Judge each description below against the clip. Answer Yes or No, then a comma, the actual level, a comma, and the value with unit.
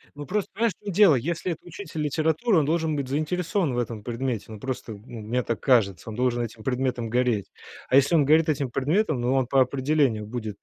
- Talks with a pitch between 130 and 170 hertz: Yes, low, 135 Hz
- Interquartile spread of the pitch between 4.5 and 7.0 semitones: Yes, average, 4.8 semitones